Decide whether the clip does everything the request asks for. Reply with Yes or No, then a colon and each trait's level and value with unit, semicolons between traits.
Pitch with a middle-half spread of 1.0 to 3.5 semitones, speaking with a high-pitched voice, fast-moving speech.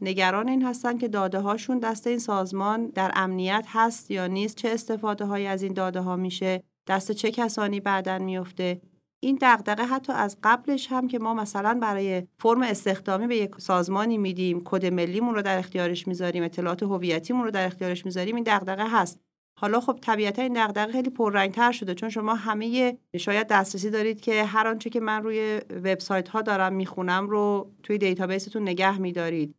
Yes: average, 3.1 semitones; high, 205 Hz; fast, 175 wpm